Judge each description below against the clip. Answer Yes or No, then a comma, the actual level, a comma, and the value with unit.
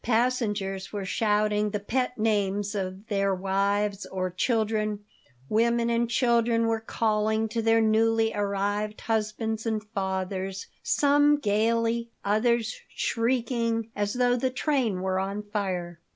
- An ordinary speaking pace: No, slow, 125 wpm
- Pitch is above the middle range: Yes, high, 215 Hz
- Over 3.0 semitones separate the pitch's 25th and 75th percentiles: No, narrow, 2.4 semitones